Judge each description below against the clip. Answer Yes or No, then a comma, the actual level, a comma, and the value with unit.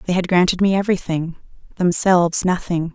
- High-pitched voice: No, medium, 180 Hz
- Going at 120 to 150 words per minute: Yes, average, 140 wpm